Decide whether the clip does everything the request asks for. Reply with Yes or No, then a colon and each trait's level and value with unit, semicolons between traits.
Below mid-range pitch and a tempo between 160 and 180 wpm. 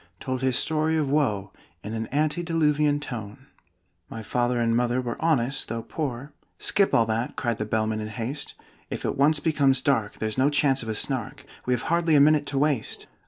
No: low, 130 Hz; average, 200 wpm